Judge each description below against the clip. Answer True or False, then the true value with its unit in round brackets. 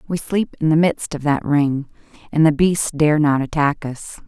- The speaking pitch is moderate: True (155 Hz)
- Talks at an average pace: False (210 wpm)